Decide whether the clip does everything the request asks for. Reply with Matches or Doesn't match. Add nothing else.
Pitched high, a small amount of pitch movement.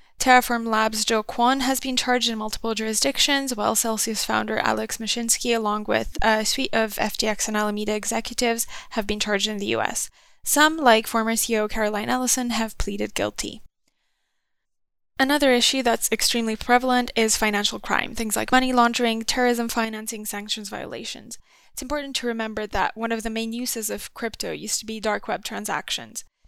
Matches